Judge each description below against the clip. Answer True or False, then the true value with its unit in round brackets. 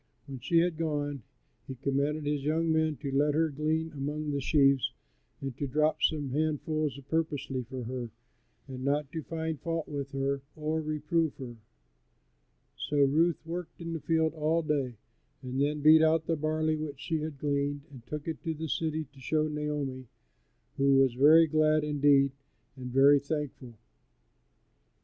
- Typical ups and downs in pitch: False (2.3 semitones)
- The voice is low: False (150 Hz)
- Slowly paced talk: False (165 wpm)